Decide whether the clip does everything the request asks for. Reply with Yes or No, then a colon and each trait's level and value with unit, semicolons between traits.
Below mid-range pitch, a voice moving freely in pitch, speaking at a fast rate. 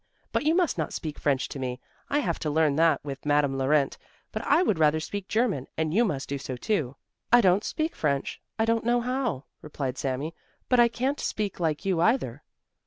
No: medium, 160 Hz; wide, 8.4 semitones; fast, 210 wpm